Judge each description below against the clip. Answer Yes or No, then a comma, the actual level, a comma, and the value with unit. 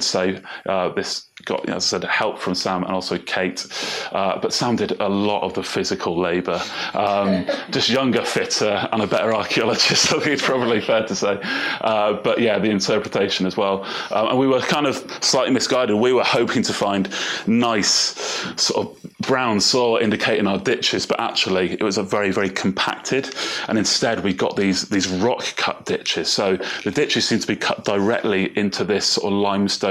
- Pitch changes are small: Yes, narrow, 1.2 semitones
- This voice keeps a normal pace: Yes, average, 195 wpm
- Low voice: Yes, low, 100 Hz